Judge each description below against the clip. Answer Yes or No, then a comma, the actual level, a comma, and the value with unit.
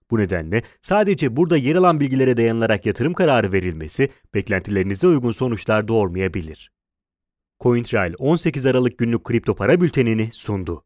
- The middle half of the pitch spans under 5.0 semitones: No, wide, 5.4 semitones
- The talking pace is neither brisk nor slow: No, slow, 125 wpm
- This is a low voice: Yes, low, 115 Hz